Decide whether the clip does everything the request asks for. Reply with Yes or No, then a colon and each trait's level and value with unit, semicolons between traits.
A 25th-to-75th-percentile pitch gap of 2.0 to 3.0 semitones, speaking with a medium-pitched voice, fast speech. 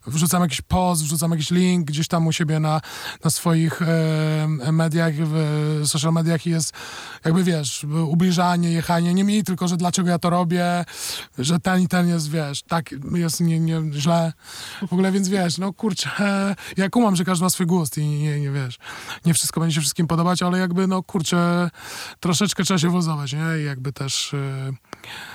Yes: narrow, 2.4 semitones; medium, 170 Hz; fast, 185 wpm